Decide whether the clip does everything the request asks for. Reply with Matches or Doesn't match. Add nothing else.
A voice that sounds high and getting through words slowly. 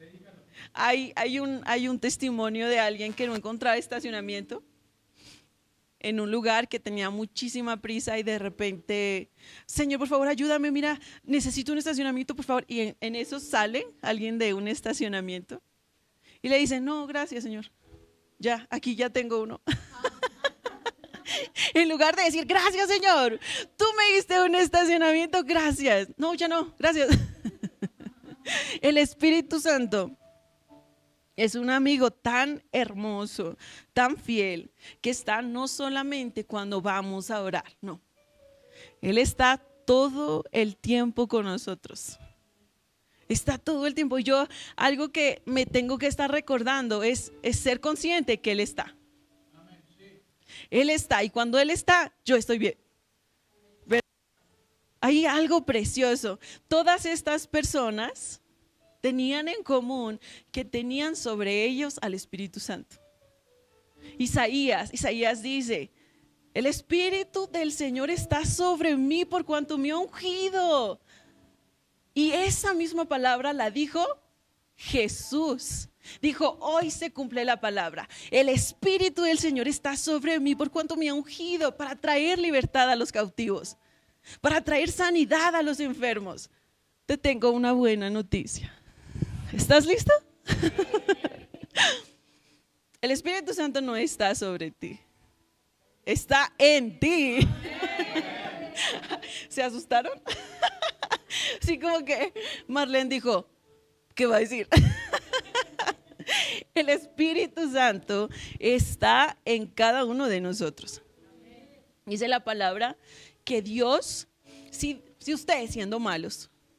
Matches